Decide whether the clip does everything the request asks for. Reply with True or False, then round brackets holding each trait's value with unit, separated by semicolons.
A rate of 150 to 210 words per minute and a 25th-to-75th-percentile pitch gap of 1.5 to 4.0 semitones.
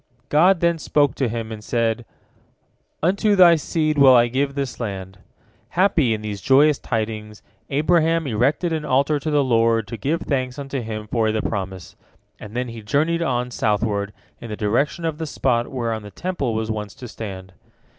False (180 wpm; 5.5 semitones)